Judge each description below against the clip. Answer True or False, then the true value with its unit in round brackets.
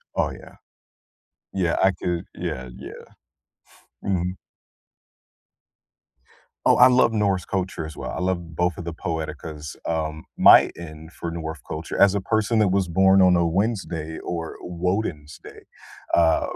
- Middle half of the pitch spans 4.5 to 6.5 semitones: False (3.0 semitones)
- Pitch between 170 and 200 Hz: False (85 Hz)